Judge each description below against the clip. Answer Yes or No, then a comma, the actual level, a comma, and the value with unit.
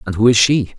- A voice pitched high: No, low, 115 Hz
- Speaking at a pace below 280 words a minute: No, fast, 305 wpm